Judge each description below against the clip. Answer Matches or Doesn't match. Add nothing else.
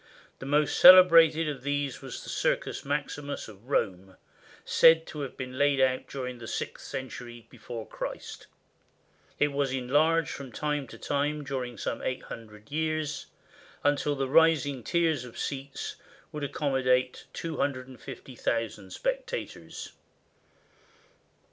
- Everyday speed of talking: Doesn't match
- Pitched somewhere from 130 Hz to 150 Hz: Matches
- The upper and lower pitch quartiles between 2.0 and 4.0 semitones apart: Matches